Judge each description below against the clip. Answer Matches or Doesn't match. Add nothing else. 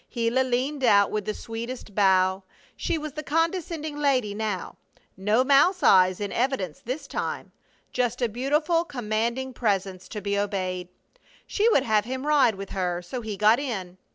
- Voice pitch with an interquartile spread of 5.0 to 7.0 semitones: Matches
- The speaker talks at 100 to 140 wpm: Doesn't match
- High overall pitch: Matches